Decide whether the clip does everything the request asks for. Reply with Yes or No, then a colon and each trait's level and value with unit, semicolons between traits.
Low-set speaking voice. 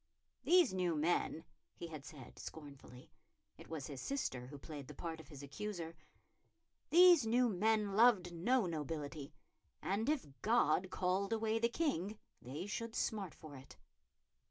No: medium, 180 Hz